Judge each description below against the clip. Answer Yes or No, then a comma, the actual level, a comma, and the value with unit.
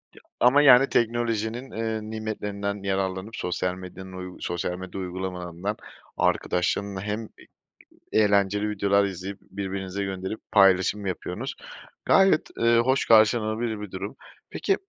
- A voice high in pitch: No, low, 100 Hz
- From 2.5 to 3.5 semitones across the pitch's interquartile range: Yes, average, 2.8 semitones